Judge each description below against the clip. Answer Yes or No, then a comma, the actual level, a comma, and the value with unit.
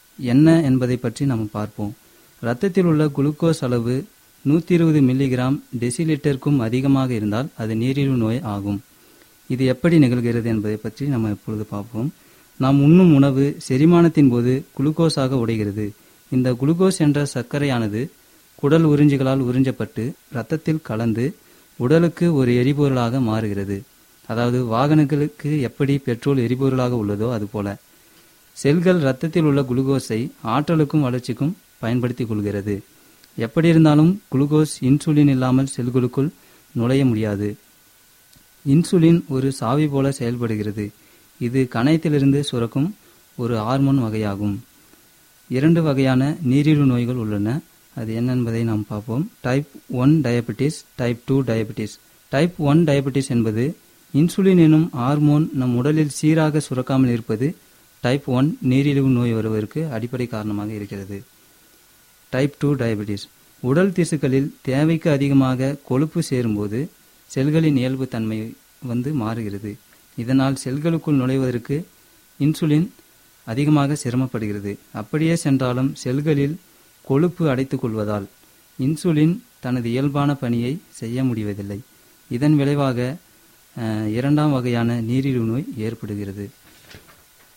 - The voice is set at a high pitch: No, low, 135 Hz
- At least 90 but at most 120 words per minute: Yes, average, 110 wpm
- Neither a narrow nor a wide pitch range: Yes, average, 4.1 semitones